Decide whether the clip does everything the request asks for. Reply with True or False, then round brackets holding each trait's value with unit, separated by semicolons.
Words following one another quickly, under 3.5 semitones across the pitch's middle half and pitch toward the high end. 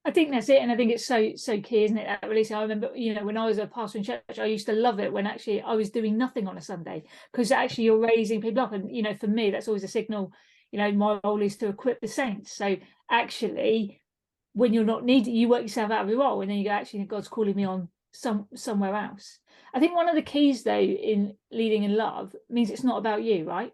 True (270 wpm; 2.4 semitones; 220 Hz)